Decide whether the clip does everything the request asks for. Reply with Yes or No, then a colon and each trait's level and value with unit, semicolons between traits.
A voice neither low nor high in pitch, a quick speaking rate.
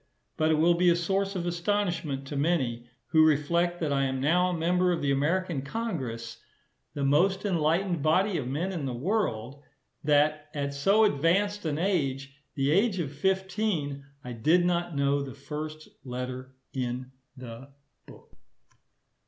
No: medium, 155 Hz; average, 160 wpm